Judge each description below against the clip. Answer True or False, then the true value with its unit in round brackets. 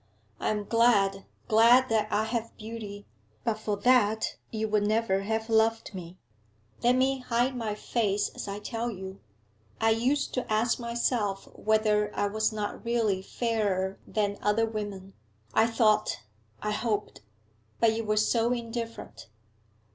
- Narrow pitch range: True (2.0 semitones)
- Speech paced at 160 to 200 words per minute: False (145 wpm)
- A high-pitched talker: True (220 Hz)